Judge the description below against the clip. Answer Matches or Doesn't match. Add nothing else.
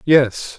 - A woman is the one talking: Doesn't match